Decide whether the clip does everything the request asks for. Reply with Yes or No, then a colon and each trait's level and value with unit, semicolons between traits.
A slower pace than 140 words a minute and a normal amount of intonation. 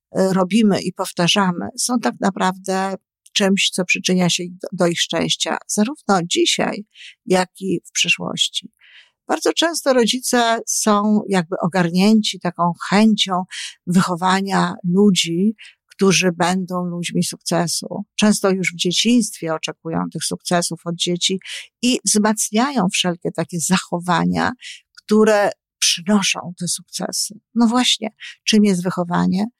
Yes: average, 115 wpm; average, 3.1 semitones